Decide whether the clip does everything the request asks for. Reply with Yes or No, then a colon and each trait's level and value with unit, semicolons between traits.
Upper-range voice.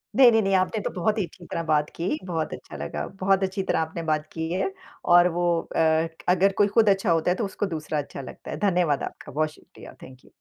No: medium, 175 Hz